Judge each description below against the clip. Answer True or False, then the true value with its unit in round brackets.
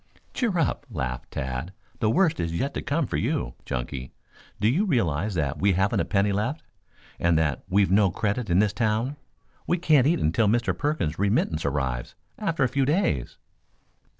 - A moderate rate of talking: True (180 wpm)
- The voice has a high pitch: False (105 Hz)